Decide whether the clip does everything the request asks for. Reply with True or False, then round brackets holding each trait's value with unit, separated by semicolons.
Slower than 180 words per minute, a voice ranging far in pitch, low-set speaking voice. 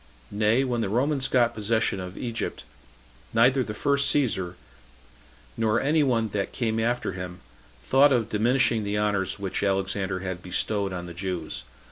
False (155 wpm; 4.2 semitones; 110 Hz)